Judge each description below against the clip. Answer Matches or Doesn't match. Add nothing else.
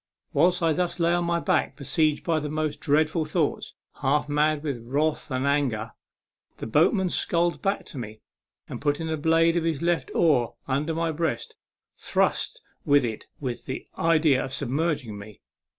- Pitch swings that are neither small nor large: Matches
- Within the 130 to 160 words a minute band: Doesn't match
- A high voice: Doesn't match